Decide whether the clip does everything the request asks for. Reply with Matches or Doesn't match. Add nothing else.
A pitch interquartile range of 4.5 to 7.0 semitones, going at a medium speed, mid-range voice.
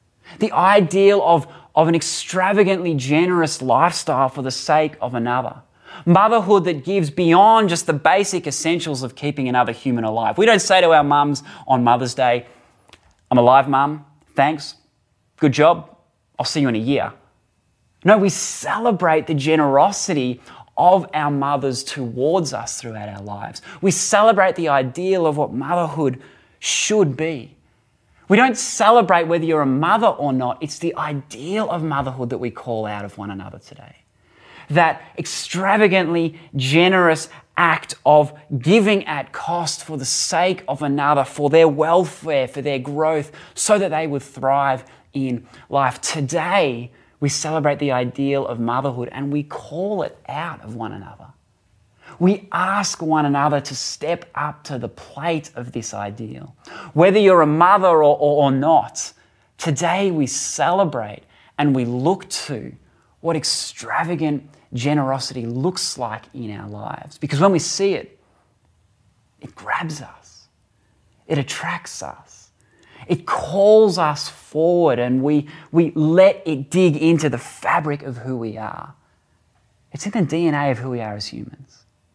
Matches